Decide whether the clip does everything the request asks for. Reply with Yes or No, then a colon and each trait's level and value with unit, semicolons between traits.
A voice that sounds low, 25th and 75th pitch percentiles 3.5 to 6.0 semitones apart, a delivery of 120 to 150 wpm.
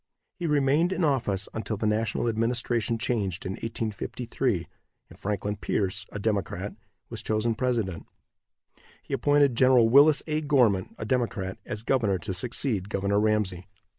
Yes: low, 110 Hz; average, 4.0 semitones; average, 140 wpm